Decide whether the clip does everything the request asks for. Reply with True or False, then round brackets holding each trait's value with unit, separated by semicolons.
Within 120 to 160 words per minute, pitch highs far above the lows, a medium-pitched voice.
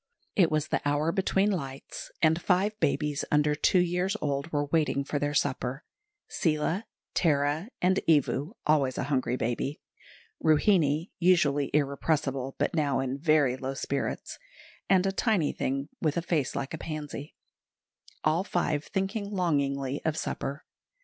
False (145 wpm; 3.6 semitones; 150 Hz)